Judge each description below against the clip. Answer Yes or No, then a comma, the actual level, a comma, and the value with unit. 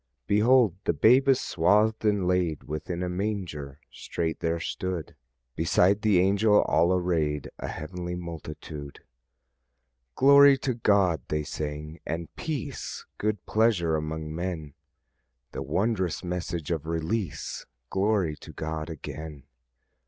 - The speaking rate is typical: No, slow, 125 wpm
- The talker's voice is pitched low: Yes, very low, 90 Hz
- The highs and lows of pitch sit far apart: No, average, 4.7 semitones